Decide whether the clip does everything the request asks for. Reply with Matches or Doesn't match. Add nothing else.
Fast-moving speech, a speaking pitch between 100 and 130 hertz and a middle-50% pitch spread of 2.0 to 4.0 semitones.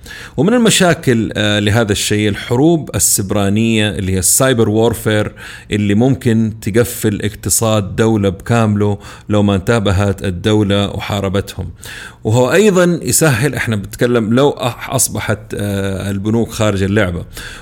Doesn't match